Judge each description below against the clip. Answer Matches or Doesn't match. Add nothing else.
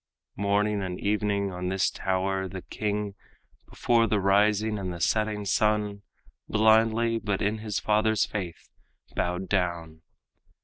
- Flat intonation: Matches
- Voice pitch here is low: Matches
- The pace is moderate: Doesn't match